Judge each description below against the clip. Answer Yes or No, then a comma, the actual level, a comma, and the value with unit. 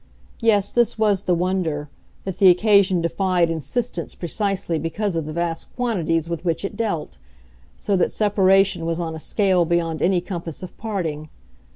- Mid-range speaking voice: Yes, medium, 180 Hz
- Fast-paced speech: No, average, 165 wpm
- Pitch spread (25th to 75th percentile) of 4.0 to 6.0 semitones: No, average, 3.3 semitones